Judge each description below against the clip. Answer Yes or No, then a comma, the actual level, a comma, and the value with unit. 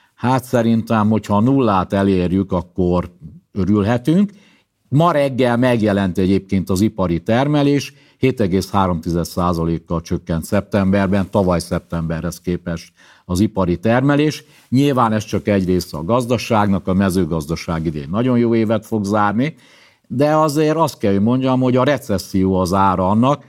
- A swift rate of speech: No, average, 130 wpm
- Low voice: Yes, low, 100 Hz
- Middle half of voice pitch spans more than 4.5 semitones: Yes, wide, 5.4 semitones